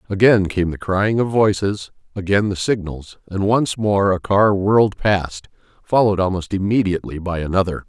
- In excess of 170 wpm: No, average, 160 wpm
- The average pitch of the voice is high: No, low, 100 Hz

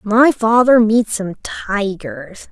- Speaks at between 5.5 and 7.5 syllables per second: No, 2.9 syllables/s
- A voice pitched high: Yes, high, 215 Hz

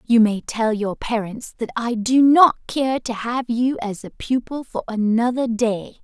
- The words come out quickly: No, average, 190 wpm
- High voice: Yes, high, 235 Hz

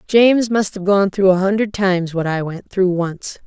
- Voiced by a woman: Yes, female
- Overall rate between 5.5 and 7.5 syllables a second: No, 4.9 syllables/s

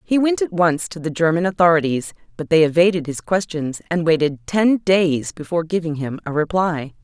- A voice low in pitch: No, medium, 170 Hz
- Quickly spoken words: No, average, 190 wpm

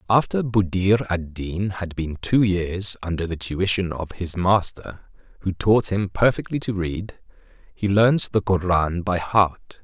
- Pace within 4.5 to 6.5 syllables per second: No, 4.0 syllables/s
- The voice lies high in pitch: No, very low, 95 Hz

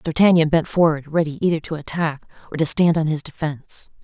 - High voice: No, medium, 160 Hz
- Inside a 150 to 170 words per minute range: No, average, 195 wpm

